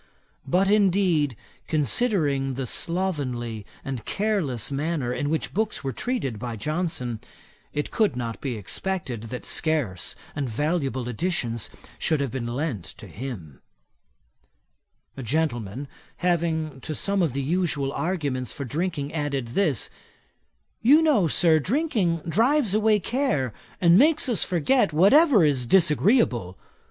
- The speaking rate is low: Yes, slow, 130 wpm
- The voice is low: No, medium, 155 Hz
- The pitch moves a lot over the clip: Yes, wide, 6.8 semitones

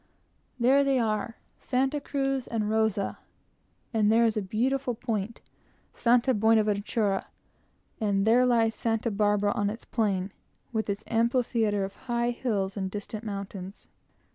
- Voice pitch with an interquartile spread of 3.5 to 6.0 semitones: No, narrow, 2.6 semitones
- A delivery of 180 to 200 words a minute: No, average, 140 wpm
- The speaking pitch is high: Yes, high, 220 Hz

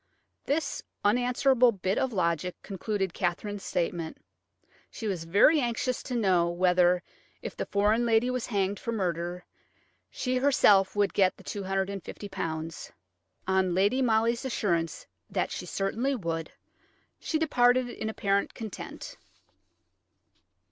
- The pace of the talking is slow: Yes, slow, 120 wpm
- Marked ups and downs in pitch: No, average, 4.9 semitones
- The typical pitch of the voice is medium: No, high, 200 Hz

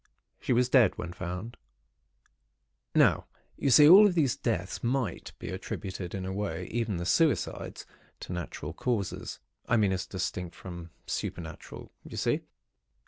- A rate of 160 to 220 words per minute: No, average, 140 wpm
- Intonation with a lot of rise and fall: Yes, wide, 5.7 semitones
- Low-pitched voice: Yes, low, 100 Hz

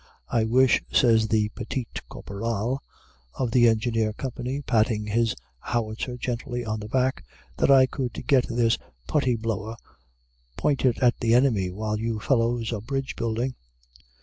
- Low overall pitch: Yes, low, 115 Hz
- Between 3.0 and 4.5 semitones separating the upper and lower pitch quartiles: No, narrow, 2.5 semitones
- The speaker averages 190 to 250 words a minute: No, average, 145 wpm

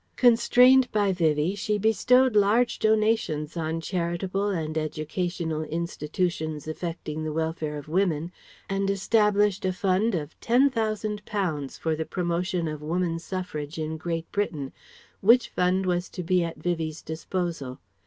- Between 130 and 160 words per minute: Yes, average, 140 wpm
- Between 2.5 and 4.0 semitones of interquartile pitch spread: No, average, 4.4 semitones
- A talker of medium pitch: Yes, medium, 175 Hz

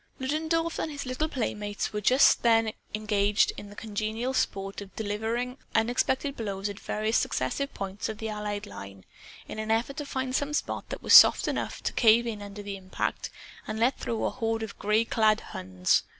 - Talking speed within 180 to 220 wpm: Yes, average, 190 wpm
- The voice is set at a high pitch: Yes, high, 220 Hz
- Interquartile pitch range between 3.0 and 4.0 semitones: Yes, average, 3.4 semitones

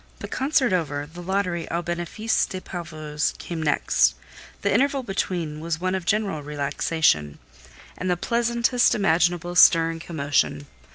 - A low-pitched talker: No, medium, 175 Hz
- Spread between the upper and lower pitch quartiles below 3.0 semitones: No, average, 3.7 semitones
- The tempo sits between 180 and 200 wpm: No, average, 150 wpm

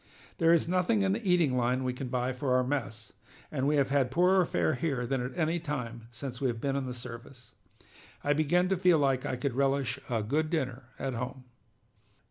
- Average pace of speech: No, fast, 215 wpm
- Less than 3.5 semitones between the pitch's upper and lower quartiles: No, average, 3.8 semitones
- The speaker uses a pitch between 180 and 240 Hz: No, low, 135 Hz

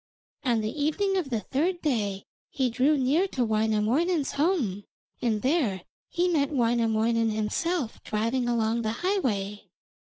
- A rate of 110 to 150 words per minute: Yes, slow, 135 wpm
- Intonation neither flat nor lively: No, wide, 5.8 semitones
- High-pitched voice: Yes, high, 240 Hz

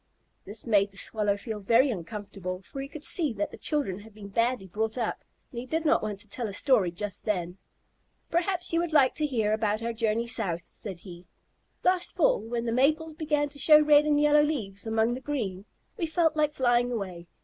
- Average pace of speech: No, fast, 215 wpm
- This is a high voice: Yes, high, 235 Hz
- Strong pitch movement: Yes, wide, 6.4 semitones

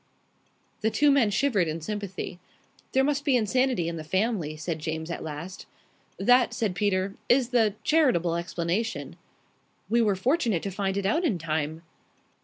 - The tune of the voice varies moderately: No, wide, 6.2 semitones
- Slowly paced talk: No, average, 160 wpm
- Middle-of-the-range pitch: No, high, 200 Hz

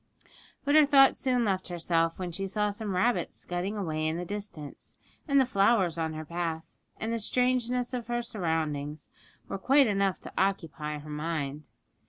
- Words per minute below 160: No, average, 175 wpm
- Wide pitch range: Yes, wide, 6.4 semitones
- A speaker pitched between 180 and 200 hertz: Yes, high, 190 Hz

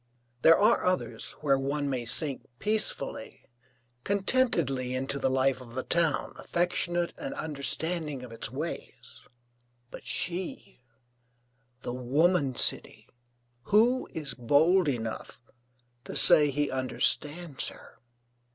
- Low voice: No, medium, 145 Hz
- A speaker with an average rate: No, slow, 115 wpm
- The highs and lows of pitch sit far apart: No, average, 4.8 semitones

